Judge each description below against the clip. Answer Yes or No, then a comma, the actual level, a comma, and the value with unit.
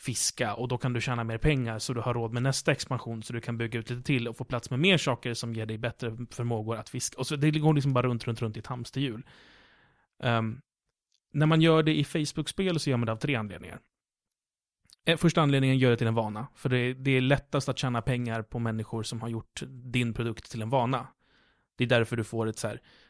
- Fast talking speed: Yes, fast, 250 wpm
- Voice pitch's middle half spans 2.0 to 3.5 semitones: Yes, average, 2.8 semitones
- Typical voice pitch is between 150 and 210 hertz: No, low, 125 Hz